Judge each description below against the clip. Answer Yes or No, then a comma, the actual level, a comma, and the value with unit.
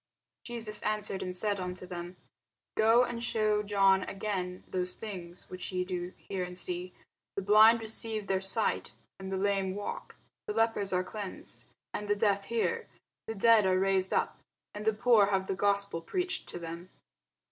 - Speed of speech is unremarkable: Yes, average, 170 wpm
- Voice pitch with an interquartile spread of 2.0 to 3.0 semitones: Yes, narrow, 2.6 semitones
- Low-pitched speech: No, high, 195 Hz